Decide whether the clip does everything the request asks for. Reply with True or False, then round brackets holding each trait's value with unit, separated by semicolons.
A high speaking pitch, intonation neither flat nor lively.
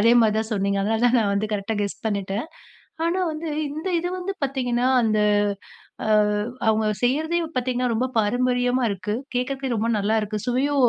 True (240 Hz; 3.7 semitones)